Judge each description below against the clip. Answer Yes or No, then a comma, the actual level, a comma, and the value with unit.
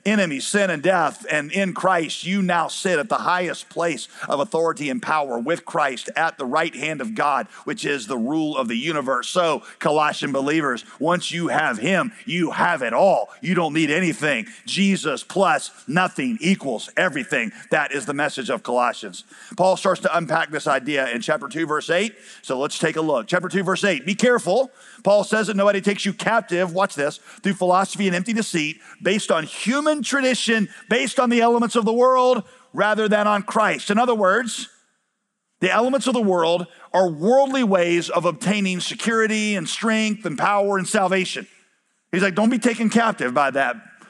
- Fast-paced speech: No, average, 190 wpm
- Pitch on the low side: No, high, 195 Hz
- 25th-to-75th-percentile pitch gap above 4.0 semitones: Yes, average, 4.6 semitones